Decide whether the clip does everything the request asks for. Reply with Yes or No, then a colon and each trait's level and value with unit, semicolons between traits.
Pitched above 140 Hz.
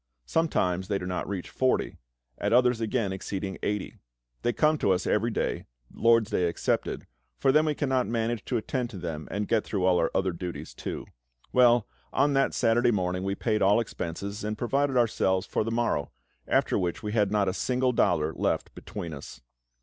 No: low, 105 Hz